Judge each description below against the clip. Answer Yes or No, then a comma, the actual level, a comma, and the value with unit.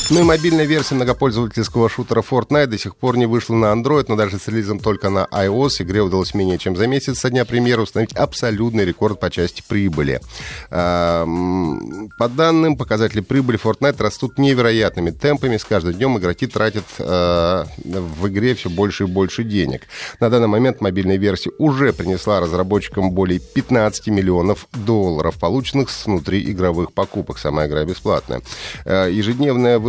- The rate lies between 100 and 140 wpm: No, average, 155 wpm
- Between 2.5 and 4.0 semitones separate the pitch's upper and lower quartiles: No, average, 4.9 semitones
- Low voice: Yes, low, 105 Hz